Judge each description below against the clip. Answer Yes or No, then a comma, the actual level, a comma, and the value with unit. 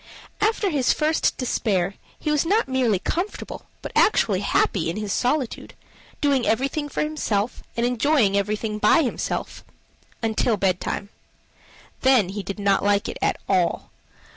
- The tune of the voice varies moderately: No, wide, 6.4 semitones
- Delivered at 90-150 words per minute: Yes, average, 140 wpm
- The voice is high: Yes, high, 230 Hz